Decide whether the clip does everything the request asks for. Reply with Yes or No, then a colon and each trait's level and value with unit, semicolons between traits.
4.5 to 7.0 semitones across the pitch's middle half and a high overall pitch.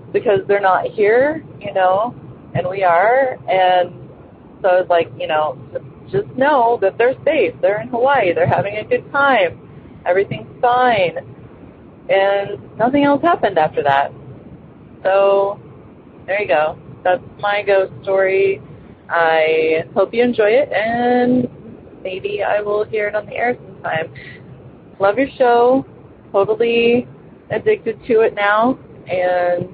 Yes: average, 5.2 semitones; high, 205 Hz